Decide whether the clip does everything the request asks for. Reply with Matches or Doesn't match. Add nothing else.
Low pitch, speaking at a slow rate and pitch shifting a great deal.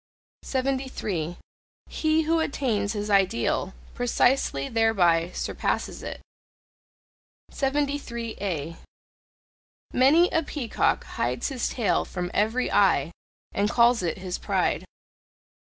Doesn't match